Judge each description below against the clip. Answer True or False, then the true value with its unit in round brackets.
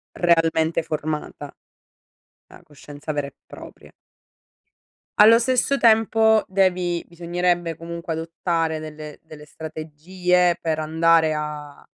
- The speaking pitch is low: False (165 Hz)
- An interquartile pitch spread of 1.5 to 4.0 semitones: True (2.5 semitones)